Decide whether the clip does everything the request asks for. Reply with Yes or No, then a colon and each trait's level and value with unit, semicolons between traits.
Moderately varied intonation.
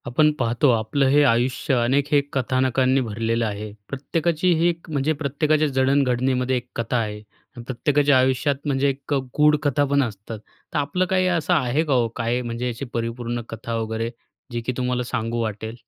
Yes: average, 3.5 semitones